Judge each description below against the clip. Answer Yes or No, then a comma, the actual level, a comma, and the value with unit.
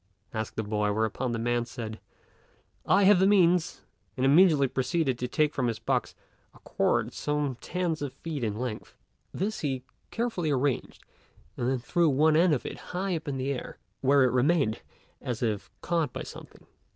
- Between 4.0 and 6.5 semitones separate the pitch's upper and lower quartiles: Yes, wide, 5.6 semitones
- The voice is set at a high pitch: No, medium, 140 Hz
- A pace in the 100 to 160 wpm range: No, average, 180 wpm